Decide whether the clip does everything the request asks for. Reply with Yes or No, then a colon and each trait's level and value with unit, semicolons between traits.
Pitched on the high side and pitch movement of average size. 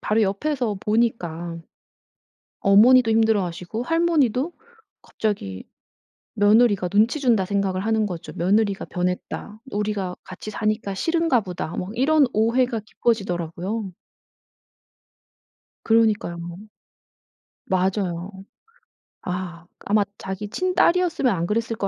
Yes: high, 210 Hz; average, 3.9 semitones